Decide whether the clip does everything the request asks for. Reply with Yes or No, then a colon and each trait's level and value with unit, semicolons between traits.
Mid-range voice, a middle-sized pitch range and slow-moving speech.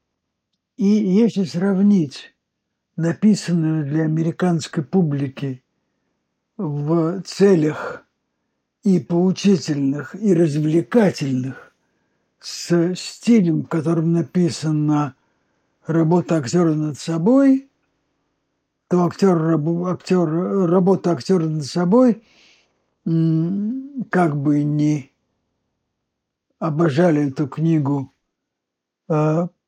Yes: medium, 170 Hz; average, 3.4 semitones; slow, 70 wpm